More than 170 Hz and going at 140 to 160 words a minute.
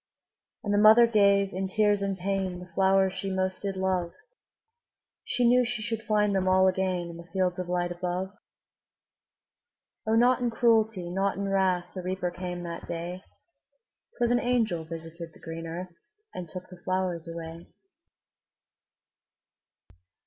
Yes: high, 190 Hz; average, 155 wpm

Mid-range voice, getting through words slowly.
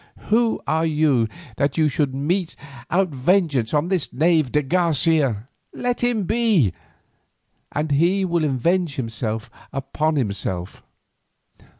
Yes: medium, 155 Hz; slow, 120 wpm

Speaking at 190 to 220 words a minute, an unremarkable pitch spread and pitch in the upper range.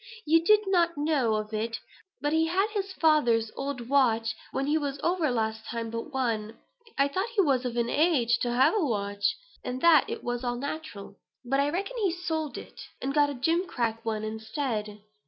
No: average, 195 wpm; wide, 5.8 semitones; very high, 270 Hz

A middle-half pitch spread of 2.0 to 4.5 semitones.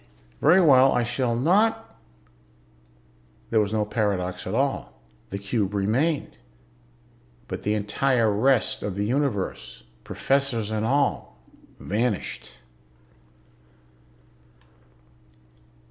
No: average, 5.3 semitones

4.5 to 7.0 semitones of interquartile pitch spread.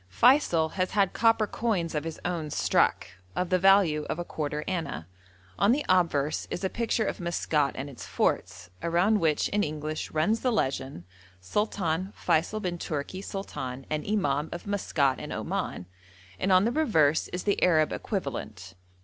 Yes: average, 4.9 semitones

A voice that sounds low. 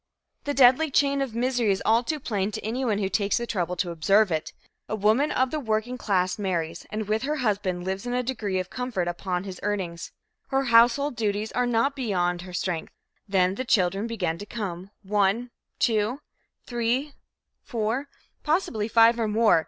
No: high, 215 Hz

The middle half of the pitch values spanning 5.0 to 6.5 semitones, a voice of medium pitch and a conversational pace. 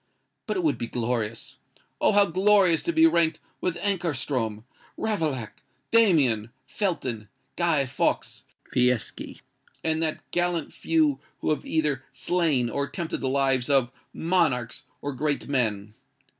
No: wide, 5.6 semitones; medium, 150 Hz; slow, 130 wpm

